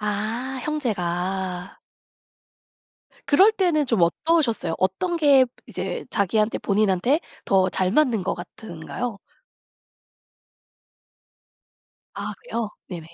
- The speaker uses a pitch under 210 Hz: No, high, 215 Hz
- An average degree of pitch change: No, wide, 7.2 semitones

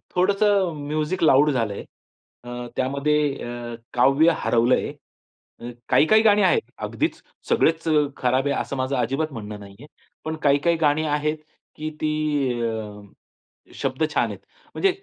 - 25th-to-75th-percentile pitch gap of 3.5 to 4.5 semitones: Yes, average, 4.2 semitones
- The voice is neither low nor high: Yes, medium, 145 Hz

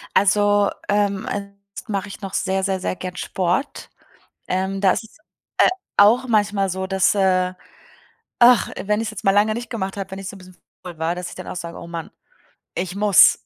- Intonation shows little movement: Yes, narrow, 1.8 semitones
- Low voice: No, high, 195 Hz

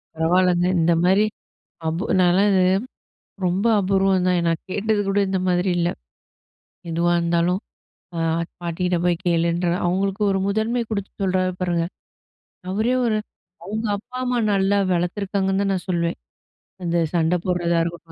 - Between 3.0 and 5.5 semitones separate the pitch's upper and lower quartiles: No, narrow, 2.4 semitones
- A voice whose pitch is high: No, medium, 180 Hz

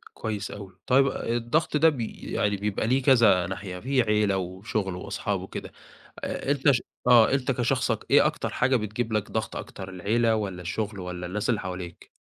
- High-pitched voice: No, low, 110 Hz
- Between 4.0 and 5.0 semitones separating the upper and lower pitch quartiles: Yes, average, 4.5 semitones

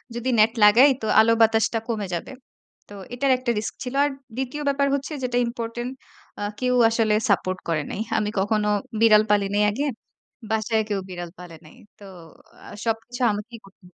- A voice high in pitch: Yes, high, 225 Hz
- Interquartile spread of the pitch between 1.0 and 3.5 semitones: Yes, average, 3.0 semitones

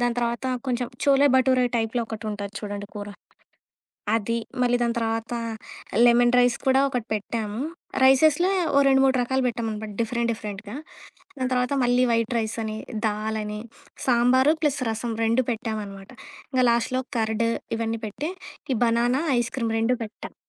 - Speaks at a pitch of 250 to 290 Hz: No, high, 235 Hz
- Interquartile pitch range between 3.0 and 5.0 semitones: No, narrow, 2.4 semitones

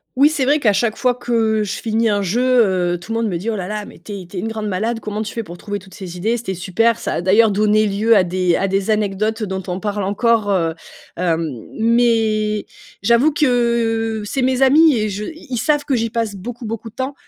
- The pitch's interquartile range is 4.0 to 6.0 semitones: No, average, 3.2 semitones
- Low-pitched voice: No, high, 215 Hz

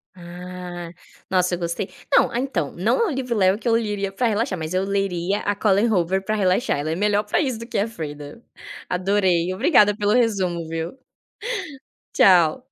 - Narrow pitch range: No, average, 3.3 semitones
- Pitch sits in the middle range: No, high, 195 Hz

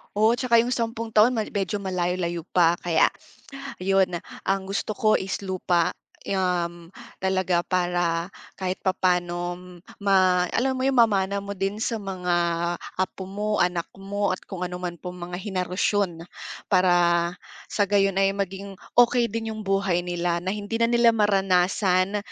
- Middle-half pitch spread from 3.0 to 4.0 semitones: No, narrow, 2.6 semitones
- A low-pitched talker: No, high, 190 Hz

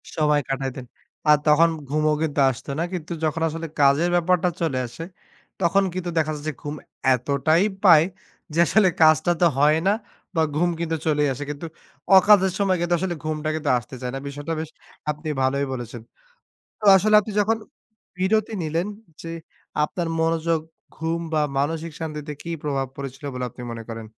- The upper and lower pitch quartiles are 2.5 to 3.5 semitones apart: Yes, average, 2.9 semitones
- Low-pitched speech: No, medium, 155 Hz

